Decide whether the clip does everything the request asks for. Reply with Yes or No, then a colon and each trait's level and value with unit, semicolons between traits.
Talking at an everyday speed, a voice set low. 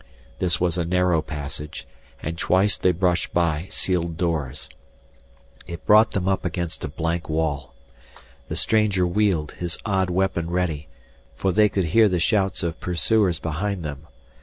Yes: average, 155 wpm; very low, 90 Hz